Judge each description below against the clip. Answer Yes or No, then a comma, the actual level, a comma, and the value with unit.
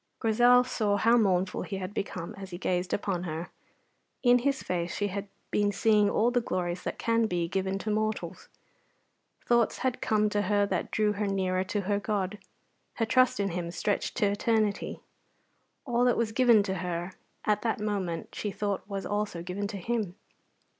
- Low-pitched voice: No, high, 205 Hz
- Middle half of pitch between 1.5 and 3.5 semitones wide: Yes, average, 2.9 semitones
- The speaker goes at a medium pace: Yes, average, 180 wpm